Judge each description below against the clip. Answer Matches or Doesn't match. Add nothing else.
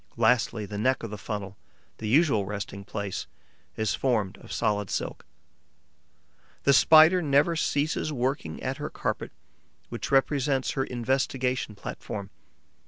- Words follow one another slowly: Matches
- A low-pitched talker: Matches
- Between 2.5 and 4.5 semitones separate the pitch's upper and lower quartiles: Doesn't match